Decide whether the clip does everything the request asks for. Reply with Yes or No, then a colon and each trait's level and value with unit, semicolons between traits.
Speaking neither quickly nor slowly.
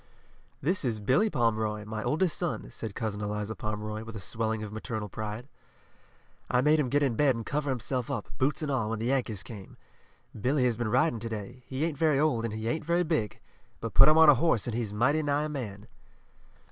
No: fast, 220 wpm